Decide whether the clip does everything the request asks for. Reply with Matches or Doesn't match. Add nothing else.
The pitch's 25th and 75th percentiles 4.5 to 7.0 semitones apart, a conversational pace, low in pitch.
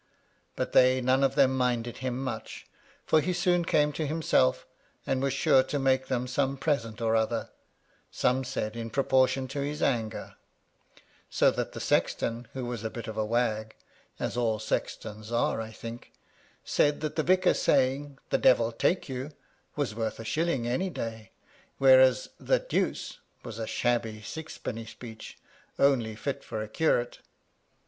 Doesn't match